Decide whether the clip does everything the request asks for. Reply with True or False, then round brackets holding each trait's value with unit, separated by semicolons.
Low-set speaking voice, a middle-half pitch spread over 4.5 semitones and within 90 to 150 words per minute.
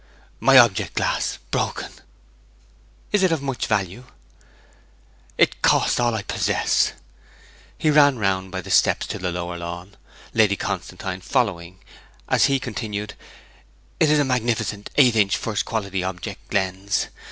True (105 Hz; 5.0 semitones; 140 wpm)